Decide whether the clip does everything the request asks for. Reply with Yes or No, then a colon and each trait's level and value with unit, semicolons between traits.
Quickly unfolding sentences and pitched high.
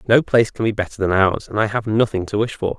No: fast, 300 wpm; low, 105 Hz